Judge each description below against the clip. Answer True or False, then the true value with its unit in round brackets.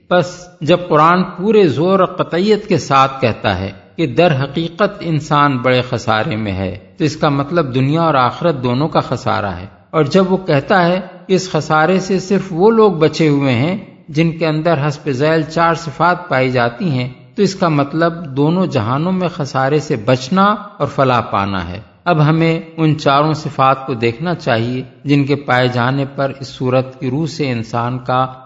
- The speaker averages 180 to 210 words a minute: True (185 wpm)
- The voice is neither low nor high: True (150 Hz)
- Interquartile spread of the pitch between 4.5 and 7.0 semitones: True (4.9 semitones)